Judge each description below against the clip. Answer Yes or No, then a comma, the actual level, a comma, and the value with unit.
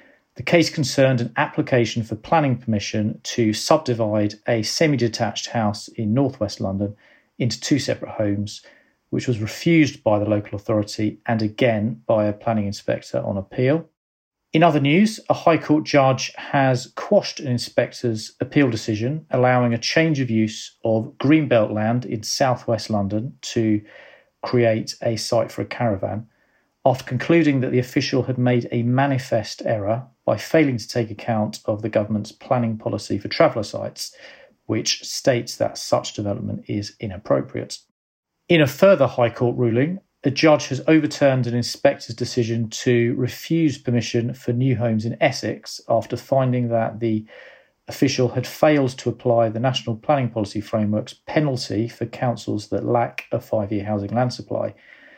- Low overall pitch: Yes, low, 120 Hz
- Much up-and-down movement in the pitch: No, average, 3.7 semitones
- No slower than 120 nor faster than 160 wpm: Yes, average, 155 wpm